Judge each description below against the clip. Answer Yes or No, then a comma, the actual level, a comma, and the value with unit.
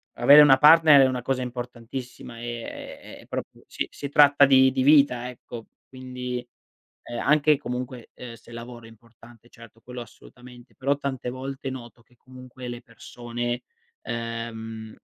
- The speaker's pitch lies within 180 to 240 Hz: No, low, 125 Hz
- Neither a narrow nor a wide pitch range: No, narrow, 2.0 semitones